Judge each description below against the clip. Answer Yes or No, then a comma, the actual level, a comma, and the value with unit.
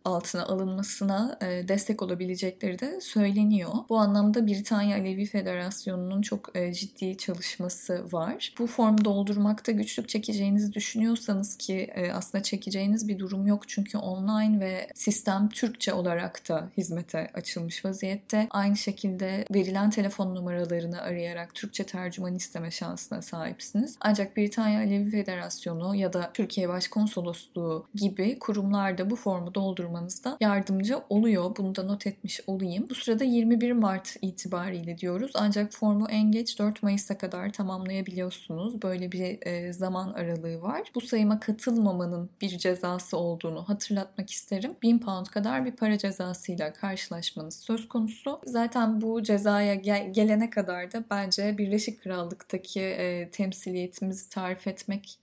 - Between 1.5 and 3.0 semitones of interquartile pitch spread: Yes, narrow, 2.6 semitones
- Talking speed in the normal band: Yes, average, 130 wpm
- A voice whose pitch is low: No, high, 200 Hz